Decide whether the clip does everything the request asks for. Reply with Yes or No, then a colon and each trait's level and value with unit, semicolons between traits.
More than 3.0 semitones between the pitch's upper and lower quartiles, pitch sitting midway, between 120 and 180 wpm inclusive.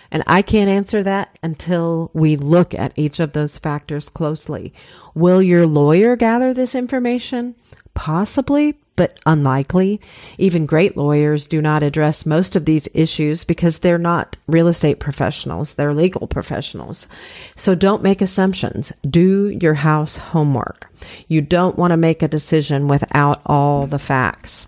Yes: average, 4.1 semitones; medium, 160 Hz; average, 150 wpm